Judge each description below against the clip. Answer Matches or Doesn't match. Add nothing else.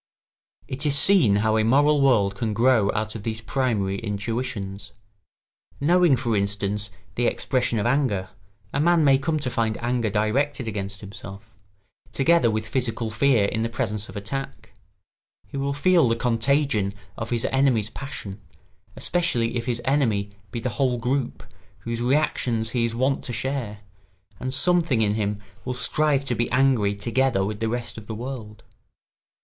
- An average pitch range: Matches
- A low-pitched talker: Matches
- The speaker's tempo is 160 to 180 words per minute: Matches